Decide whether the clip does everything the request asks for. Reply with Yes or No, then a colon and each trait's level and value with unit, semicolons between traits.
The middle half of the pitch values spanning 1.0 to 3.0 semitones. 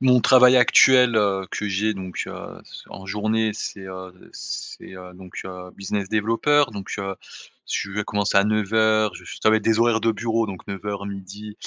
Yes: narrow, 2.4 semitones